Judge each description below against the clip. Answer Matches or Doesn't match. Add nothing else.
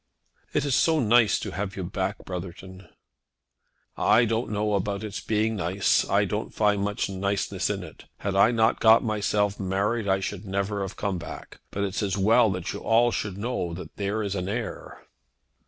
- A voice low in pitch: Matches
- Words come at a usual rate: Matches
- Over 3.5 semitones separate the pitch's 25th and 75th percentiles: Doesn't match